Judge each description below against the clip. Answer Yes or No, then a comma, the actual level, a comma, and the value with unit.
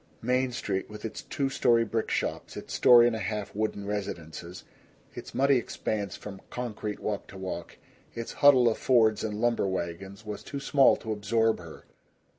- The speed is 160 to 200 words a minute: Yes, average, 175 wpm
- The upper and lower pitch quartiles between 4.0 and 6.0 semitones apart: No, average, 3.1 semitones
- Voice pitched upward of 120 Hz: No, low, 110 Hz